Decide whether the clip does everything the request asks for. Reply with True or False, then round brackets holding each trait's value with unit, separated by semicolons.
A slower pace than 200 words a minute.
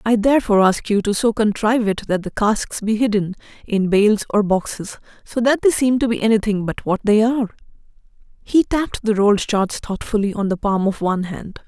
False (205 wpm)